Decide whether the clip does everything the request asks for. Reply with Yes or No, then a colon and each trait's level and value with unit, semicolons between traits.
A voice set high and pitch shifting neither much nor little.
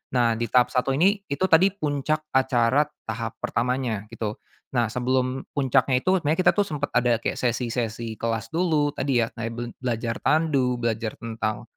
No: low, 125 Hz; average, 3.7 semitones